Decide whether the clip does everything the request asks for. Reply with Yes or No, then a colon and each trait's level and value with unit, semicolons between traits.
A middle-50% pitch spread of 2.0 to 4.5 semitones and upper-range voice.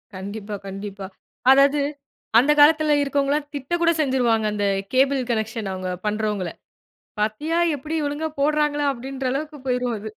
No: wide, 5.4 semitones; very high, 265 Hz